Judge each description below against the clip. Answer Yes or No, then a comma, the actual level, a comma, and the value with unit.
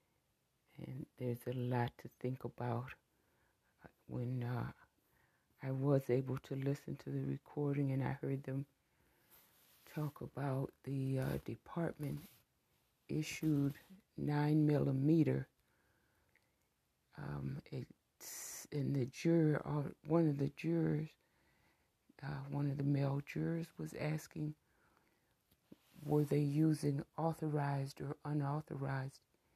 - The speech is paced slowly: Yes, slow, 105 wpm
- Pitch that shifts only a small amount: Yes, narrow, 2.3 semitones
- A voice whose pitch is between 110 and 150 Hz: Yes, medium, 140 Hz